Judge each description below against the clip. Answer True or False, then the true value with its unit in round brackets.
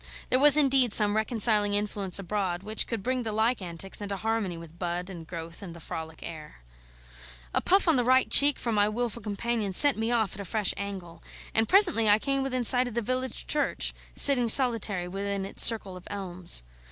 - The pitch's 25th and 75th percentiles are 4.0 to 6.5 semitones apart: True (4.5 semitones)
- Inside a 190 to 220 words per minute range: True (200 wpm)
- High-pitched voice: True (210 Hz)